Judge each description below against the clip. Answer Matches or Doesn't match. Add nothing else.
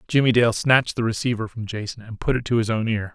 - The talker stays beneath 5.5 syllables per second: Doesn't match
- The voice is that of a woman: Doesn't match